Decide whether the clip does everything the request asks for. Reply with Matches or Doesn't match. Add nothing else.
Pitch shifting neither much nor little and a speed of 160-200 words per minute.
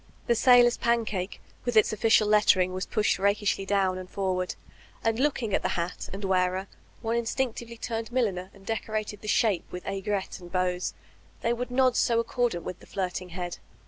Matches